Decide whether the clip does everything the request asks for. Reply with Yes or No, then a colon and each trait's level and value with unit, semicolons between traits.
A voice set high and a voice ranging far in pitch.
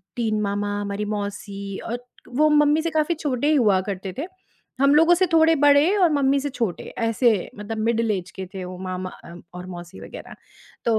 Yes: high, 230 Hz; wide, 6.5 semitones